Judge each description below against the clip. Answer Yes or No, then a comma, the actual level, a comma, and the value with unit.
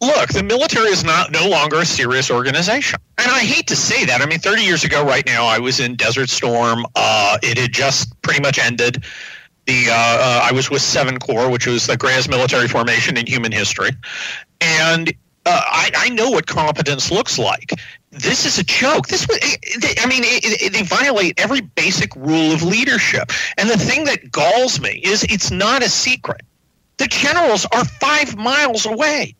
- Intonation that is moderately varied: No, wide, 5.8 semitones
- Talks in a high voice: No, low, 135 Hz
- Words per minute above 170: Yes, average, 195 wpm